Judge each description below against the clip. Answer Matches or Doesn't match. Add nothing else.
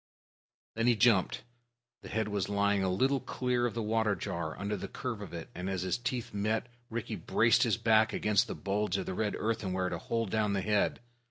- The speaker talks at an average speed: Doesn't match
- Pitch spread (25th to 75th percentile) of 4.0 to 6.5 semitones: Doesn't match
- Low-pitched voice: Matches